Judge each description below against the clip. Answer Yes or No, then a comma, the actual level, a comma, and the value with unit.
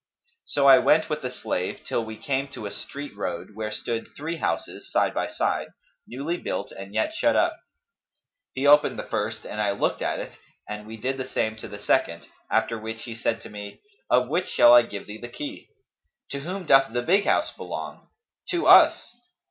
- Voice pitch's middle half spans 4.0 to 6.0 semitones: Yes, average, 4.6 semitones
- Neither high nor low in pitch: No, low, 120 Hz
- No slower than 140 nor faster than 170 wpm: No, fast, 205 wpm